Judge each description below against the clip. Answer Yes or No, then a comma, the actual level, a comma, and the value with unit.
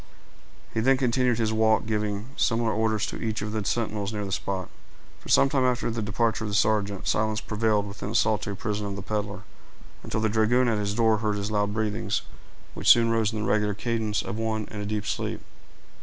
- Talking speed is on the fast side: Yes, fast, 215 wpm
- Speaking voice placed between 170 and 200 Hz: No, low, 110 Hz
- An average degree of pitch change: No, narrow, 1.5 semitones